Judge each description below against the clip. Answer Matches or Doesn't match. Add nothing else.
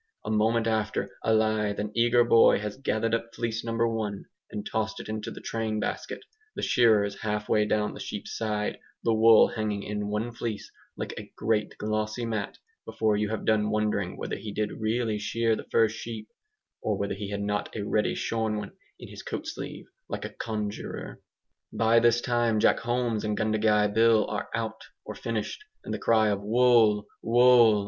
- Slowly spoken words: Doesn't match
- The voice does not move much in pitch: Matches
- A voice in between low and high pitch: Doesn't match